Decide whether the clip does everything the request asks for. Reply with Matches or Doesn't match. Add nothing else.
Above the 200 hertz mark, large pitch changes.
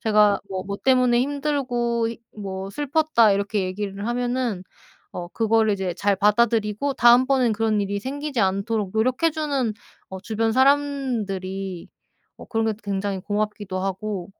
Doesn't match